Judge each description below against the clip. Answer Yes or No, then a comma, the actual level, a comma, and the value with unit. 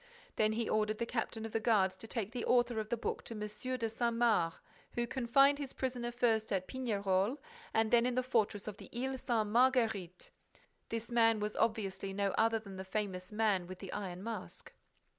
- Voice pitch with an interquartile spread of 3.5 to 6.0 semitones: No, average, 2.8 semitones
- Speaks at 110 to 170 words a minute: No, average, 200 wpm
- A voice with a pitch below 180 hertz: No, high, 220 Hz